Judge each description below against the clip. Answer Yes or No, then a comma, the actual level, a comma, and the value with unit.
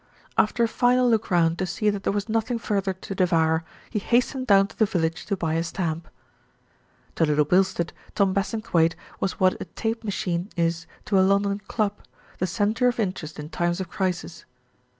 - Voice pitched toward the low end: No, high, 190 Hz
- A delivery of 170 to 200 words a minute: Yes, average, 190 wpm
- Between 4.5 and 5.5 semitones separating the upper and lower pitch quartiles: No, average, 3.9 semitones